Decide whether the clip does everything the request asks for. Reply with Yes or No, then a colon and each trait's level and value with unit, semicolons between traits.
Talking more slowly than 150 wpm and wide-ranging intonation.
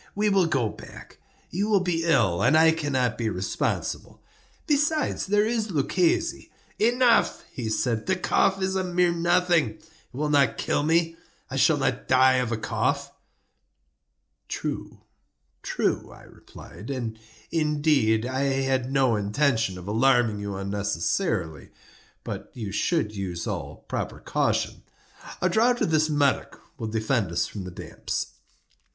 Yes: average, 140 wpm; wide, 7.8 semitones